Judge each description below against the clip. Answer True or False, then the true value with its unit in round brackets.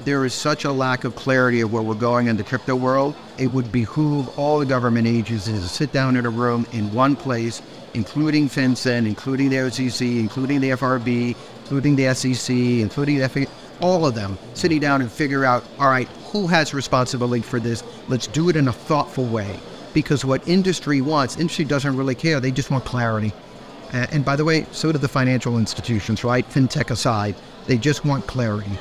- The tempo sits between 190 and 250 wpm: True (200 wpm)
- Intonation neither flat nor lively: True (3.0 semitones)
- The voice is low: True (130 Hz)